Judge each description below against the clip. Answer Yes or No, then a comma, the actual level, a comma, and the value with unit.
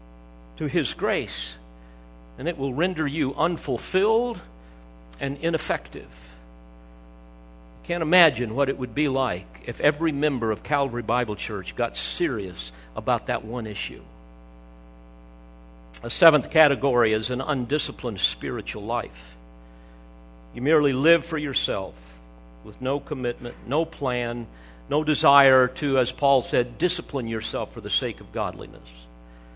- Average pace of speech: No, slow, 125 wpm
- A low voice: Yes, low, 110 Hz